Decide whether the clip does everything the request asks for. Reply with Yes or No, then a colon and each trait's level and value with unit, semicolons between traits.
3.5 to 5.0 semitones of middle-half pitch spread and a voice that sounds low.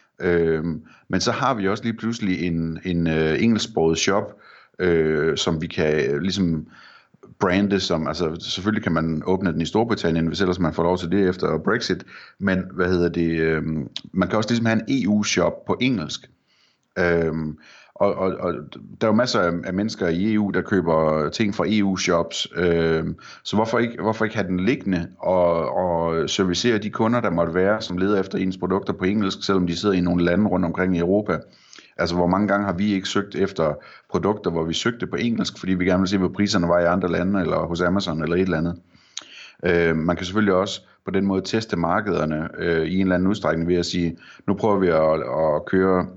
No: average, 3.0 semitones; very low, 90 Hz